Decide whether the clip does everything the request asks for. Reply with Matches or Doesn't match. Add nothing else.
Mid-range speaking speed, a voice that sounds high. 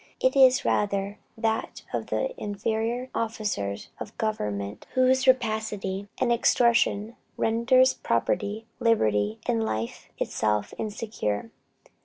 Doesn't match